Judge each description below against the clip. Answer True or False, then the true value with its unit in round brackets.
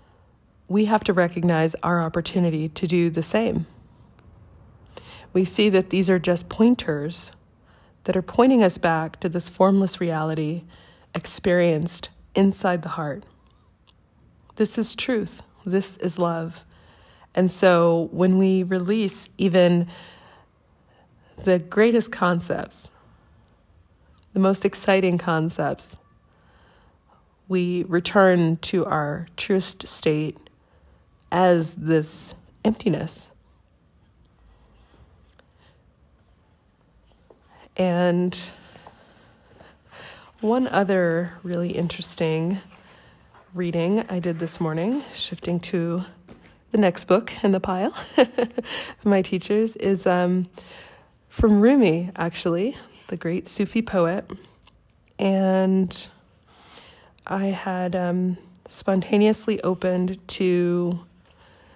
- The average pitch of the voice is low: False (180 Hz)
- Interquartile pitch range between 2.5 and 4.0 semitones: True (3.1 semitones)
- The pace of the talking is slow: True (90 wpm)